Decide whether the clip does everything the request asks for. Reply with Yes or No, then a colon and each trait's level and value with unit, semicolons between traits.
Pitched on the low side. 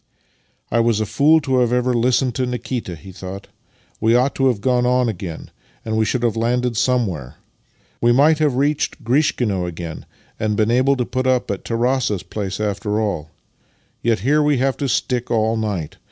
Yes: low, 120 Hz